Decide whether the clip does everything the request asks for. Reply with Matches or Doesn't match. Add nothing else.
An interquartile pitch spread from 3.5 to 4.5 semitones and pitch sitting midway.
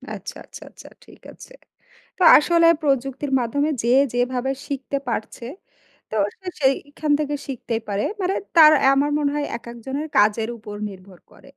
Doesn't match